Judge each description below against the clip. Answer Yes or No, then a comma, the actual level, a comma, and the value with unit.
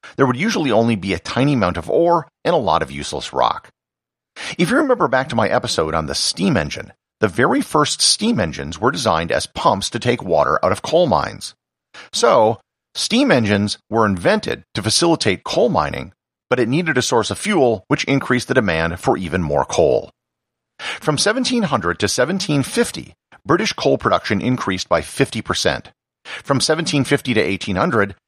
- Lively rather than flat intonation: Yes, wide, 7.2 semitones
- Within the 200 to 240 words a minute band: No, average, 170 wpm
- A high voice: No, low, 135 Hz